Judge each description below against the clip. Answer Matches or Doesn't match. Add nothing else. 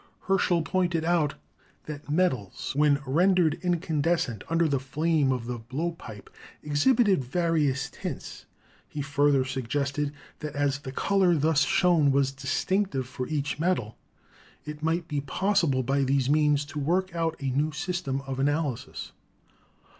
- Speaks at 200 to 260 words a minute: Doesn't match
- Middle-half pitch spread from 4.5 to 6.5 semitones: Doesn't match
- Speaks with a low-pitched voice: Doesn't match